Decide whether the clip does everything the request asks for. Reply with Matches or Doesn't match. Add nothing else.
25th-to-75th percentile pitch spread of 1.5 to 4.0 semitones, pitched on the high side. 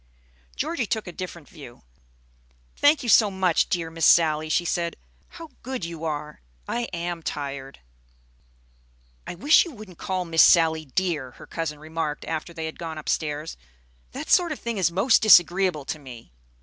Doesn't match